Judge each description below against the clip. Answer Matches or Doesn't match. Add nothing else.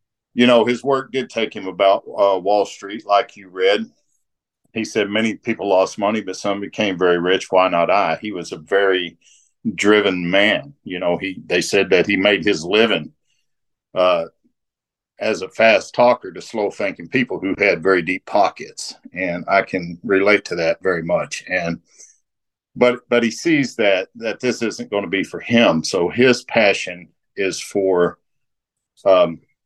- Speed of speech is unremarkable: Matches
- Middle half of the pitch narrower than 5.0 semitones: Matches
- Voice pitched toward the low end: Matches